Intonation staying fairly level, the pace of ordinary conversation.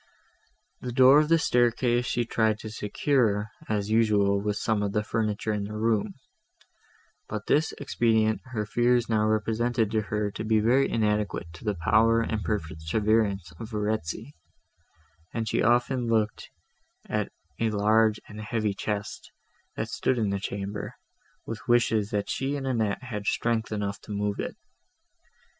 Yes: narrow, 2.0 semitones; average, 155 wpm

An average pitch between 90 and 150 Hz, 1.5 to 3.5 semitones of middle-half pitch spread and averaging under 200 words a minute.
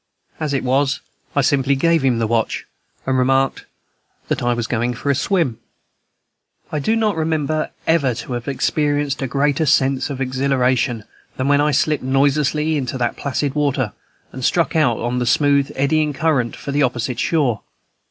Yes: medium, 140 Hz; average, 2.7 semitones; average, 175 wpm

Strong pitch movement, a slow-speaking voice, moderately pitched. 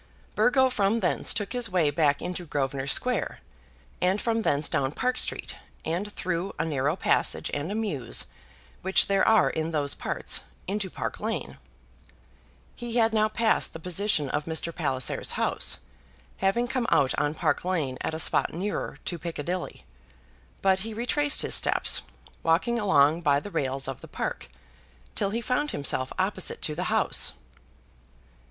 No: wide, 6.3 semitones; average, 160 wpm; medium, 180 Hz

